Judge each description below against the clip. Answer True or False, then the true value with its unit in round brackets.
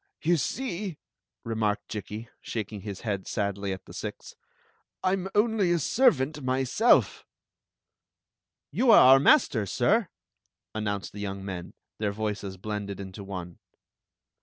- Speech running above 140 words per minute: False (135 wpm)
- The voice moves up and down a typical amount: False (9.0 semitones)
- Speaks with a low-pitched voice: True (110 Hz)